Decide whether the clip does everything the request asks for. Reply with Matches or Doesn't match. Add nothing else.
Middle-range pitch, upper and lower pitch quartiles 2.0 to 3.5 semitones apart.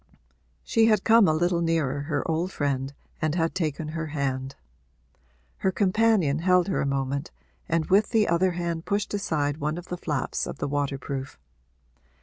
Doesn't match